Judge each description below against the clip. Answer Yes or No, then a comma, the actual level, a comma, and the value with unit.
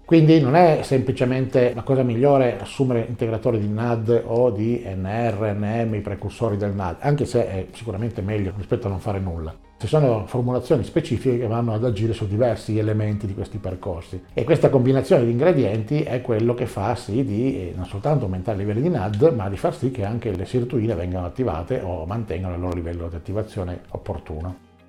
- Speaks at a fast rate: Yes, fast, 190 wpm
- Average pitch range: Yes, average, 4.3 semitones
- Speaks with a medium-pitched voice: No, low, 115 Hz